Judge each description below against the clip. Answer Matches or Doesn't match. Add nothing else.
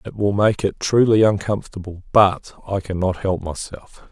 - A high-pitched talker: Doesn't match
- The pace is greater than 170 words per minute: Doesn't match